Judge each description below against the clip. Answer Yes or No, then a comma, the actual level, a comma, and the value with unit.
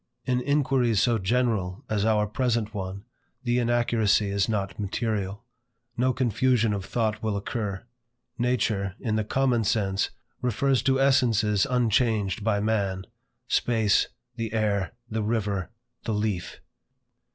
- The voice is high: No, low, 110 Hz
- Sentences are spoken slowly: Yes, slow, 130 wpm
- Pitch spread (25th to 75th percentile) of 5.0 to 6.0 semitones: No, average, 3.1 semitones